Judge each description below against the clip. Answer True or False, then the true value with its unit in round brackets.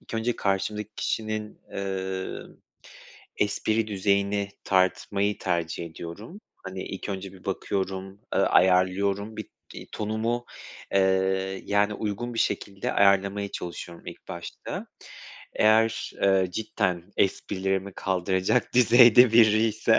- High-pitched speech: False (100 Hz)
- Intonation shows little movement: True (2.3 semitones)